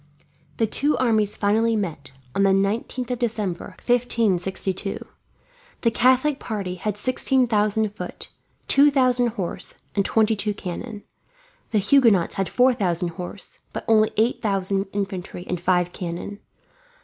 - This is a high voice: Yes, high, 210 Hz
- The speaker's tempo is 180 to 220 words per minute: No, slow, 135 wpm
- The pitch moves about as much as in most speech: Yes, average, 3.6 semitones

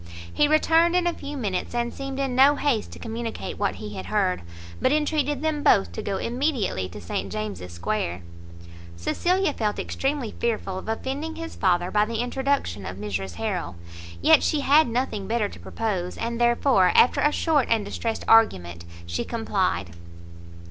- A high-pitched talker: Yes, high, 225 Hz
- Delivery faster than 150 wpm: Yes, average, 170 wpm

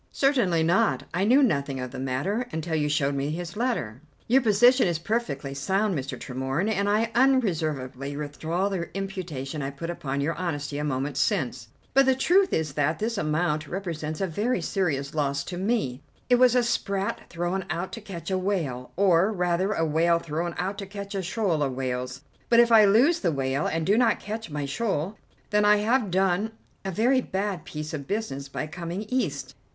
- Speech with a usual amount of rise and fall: No, wide, 6.1 semitones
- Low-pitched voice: No, medium, 175 Hz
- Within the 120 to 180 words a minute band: No, average, 195 wpm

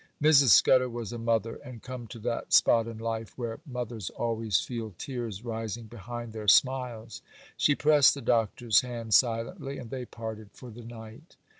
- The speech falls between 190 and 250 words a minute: No, average, 170 wpm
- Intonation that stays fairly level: Yes, narrow, 2.0 semitones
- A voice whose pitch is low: Yes, low, 115 Hz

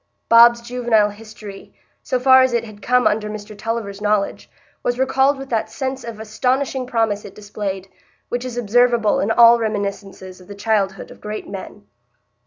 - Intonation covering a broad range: No, average, 3.0 semitones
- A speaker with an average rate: Yes, average, 170 wpm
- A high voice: Yes, high, 220 Hz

